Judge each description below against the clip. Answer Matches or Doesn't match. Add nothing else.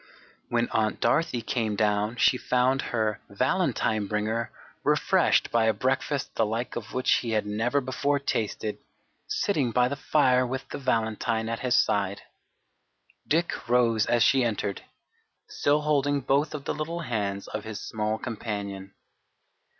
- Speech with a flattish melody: Doesn't match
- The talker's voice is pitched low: Matches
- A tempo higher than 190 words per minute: Doesn't match